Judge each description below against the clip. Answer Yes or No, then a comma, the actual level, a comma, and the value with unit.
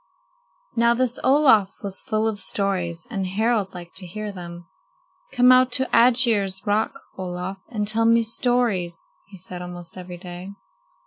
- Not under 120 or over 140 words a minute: No, average, 150 wpm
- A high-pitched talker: Yes, high, 200 Hz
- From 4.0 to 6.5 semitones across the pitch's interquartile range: Yes, average, 4.4 semitones